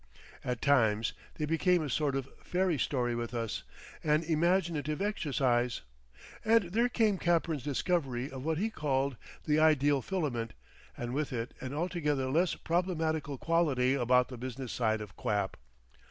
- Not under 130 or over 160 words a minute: Yes, average, 150 wpm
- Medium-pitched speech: Yes, medium, 145 Hz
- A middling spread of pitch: Yes, average, 5.0 semitones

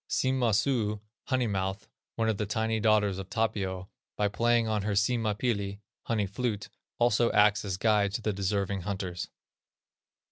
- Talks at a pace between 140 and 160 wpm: Yes, average, 155 wpm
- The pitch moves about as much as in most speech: No, narrow, 2.2 semitones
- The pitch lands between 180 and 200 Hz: No, low, 105 Hz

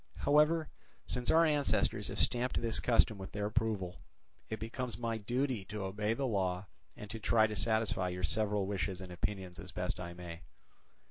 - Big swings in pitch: No, average, 3.6 semitones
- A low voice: Yes, low, 105 Hz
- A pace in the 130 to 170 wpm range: No, average, 180 wpm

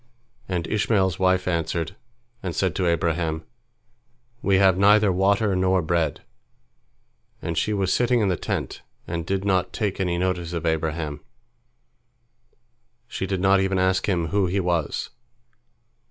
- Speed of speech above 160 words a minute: No, average, 140 wpm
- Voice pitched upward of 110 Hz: No, very low, 95 Hz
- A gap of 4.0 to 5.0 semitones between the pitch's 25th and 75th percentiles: No, narrow, 2.5 semitones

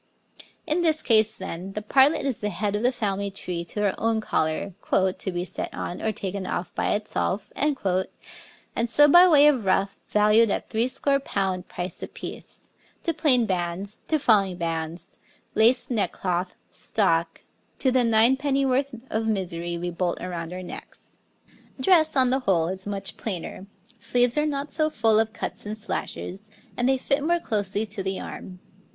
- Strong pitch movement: Yes, wide, 5.7 semitones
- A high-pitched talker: Yes, high, 210 Hz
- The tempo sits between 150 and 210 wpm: Yes, average, 170 wpm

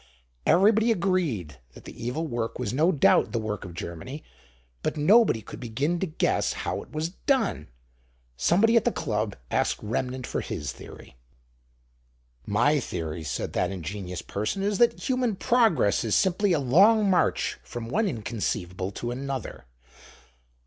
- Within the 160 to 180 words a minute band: No, average, 150 wpm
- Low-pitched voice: Yes, low, 130 Hz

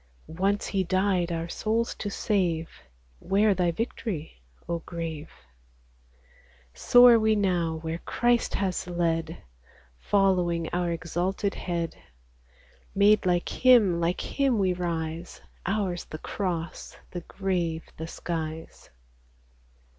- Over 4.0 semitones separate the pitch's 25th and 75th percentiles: No, average, 3.2 semitones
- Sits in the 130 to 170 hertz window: No, medium, 180 Hz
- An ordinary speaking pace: No, slow, 115 wpm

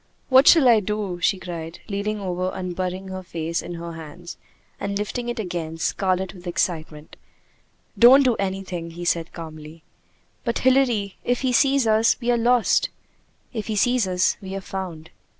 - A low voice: No, high, 190 Hz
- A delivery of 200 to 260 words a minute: No, average, 170 wpm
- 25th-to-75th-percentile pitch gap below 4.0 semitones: No, average, 4.9 semitones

